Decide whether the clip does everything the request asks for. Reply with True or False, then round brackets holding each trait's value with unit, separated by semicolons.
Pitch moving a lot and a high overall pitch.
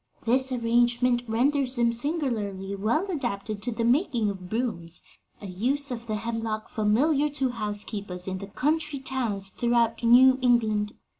False (3.7 semitones; 235 Hz)